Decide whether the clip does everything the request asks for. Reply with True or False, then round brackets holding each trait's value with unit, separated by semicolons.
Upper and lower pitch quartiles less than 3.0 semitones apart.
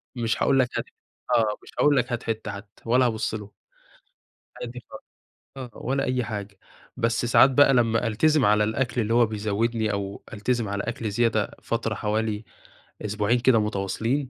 True (2.6 semitones)